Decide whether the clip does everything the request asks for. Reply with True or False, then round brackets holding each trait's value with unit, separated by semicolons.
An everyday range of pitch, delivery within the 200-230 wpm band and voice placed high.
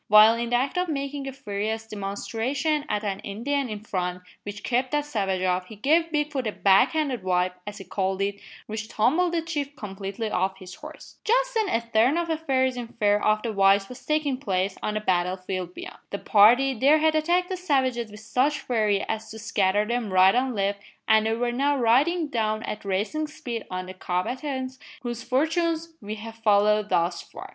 False (5.7 semitones; 205 wpm; 225 Hz)